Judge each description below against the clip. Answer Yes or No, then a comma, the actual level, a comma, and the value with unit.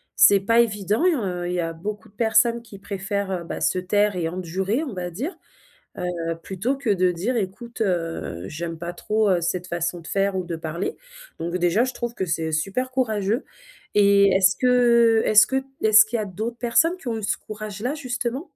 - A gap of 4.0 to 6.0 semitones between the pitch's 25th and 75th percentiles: Yes, average, 4.7 semitones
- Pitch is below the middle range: No, high, 200 Hz